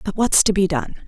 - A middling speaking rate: No, fast, 280 wpm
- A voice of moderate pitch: No, high, 195 Hz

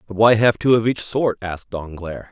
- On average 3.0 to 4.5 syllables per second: No, 5.2 syllables/s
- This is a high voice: No, low, 105 Hz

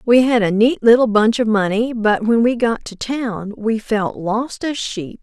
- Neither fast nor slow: No, fast, 220 wpm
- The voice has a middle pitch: No, high, 225 Hz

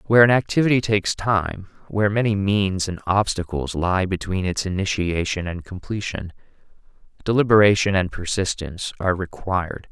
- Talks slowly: Yes, slow, 125 wpm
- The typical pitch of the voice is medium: No, very low, 95 Hz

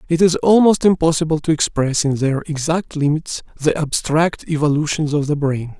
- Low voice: No, medium, 155 Hz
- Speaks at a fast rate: No, average, 165 wpm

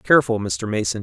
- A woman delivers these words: No, male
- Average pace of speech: Yes, average, 175 wpm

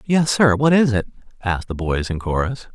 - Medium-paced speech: No, fast, 220 wpm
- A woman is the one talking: No, male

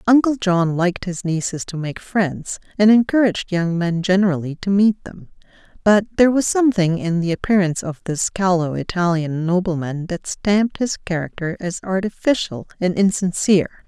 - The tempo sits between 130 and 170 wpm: Yes, average, 155 wpm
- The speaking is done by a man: No, female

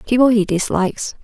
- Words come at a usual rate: Yes, average, 145 wpm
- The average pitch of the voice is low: No, high, 220 Hz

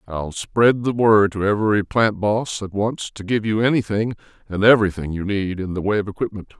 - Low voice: Yes, low, 105 Hz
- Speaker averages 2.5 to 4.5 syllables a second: No, 5.3 syllables/s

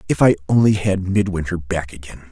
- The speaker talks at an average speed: Yes, average, 180 wpm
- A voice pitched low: Yes, very low, 90 Hz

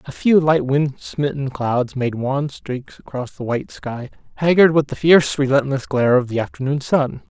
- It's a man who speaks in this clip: Yes, male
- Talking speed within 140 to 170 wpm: No, average, 190 wpm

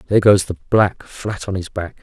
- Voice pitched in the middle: No, very low, 95 Hz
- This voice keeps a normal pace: No, fast, 240 wpm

